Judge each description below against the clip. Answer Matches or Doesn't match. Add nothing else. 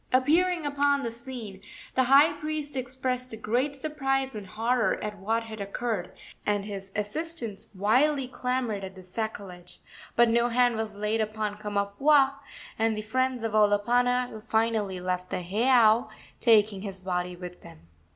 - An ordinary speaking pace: Matches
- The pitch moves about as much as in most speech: Matches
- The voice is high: Matches